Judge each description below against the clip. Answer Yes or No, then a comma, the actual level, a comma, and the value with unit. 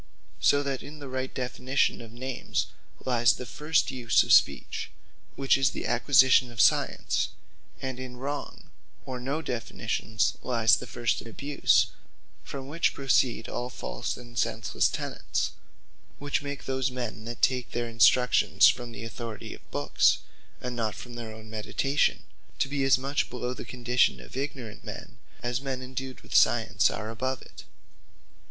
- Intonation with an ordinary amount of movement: No, narrow, 2.2 semitones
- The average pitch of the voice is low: Yes, low, 125 Hz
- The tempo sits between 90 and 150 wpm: No, average, 160 wpm